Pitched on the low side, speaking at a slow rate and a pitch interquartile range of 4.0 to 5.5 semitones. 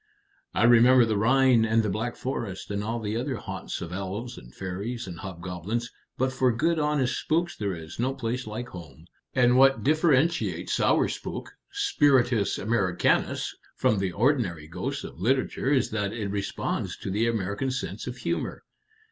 No: low, 115 Hz; average, 165 wpm; average, 4.9 semitones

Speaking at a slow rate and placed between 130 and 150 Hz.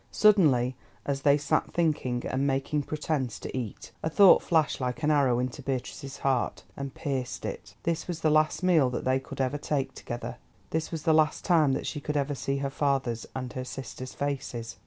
No: average, 200 wpm; medium, 140 Hz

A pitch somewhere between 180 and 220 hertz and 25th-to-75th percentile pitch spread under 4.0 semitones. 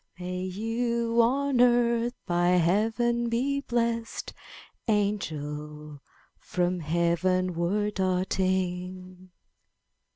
No: high, 190 Hz; average, 4.6 semitones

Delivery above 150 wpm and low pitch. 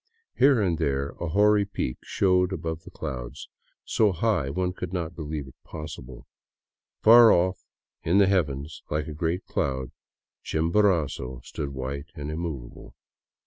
No: average, 145 wpm; very low, 80 Hz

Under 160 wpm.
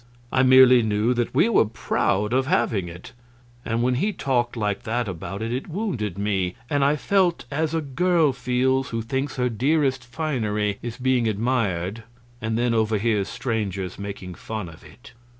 No: average, 170 wpm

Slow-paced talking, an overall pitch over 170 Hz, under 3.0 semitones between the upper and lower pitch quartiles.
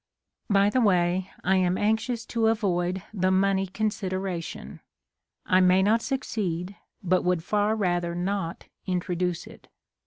Yes: slow, 130 wpm; high, 190 Hz; narrow, 2.6 semitones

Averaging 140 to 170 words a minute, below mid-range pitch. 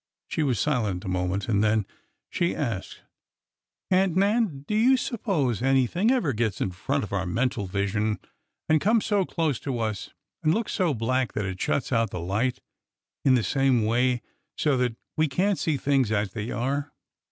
No: average, 180 wpm; low, 130 Hz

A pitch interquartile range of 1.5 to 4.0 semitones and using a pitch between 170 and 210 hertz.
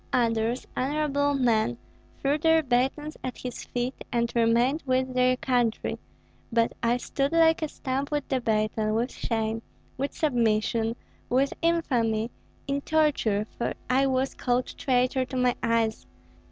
No: average, 3.2 semitones; very high, 250 Hz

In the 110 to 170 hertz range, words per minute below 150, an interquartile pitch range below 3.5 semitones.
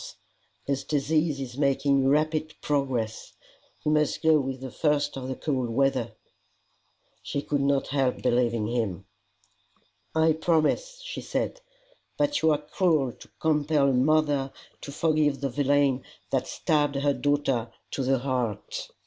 Yes: medium, 140 Hz; average, 140 wpm; narrow, 2.5 semitones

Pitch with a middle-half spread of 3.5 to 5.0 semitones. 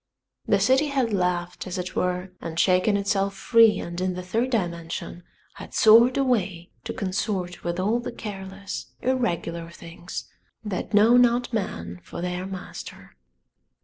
Yes: average, 4.2 semitones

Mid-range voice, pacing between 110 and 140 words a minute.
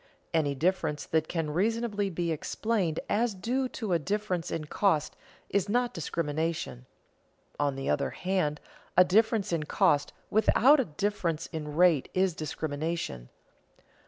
Yes: medium, 170 Hz; slow, 135 wpm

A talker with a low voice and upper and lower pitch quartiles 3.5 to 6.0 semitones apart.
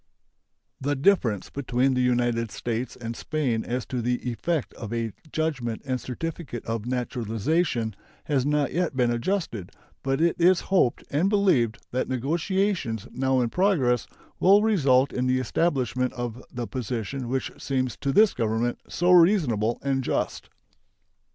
Yes: low, 130 Hz; average, 5.0 semitones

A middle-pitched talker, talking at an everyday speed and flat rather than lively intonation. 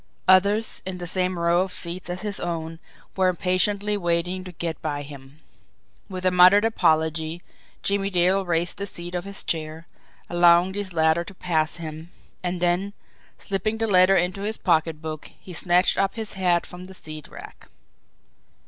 Yes: medium, 180 Hz; average, 165 wpm; narrow, 2.3 semitones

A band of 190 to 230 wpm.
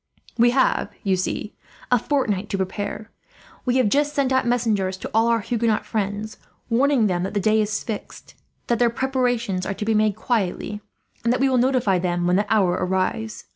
Yes: average, 195 wpm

